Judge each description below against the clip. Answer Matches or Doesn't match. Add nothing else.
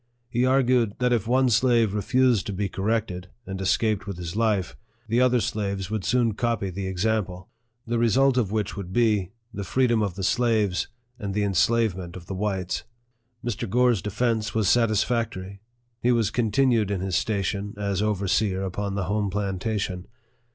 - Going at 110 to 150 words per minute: Doesn't match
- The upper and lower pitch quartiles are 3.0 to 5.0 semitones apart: Matches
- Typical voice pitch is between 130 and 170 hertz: Doesn't match